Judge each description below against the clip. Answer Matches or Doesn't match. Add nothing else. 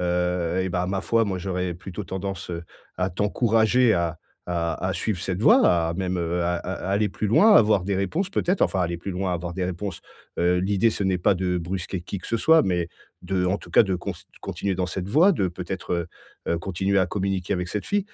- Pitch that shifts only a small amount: Matches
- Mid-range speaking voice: Doesn't match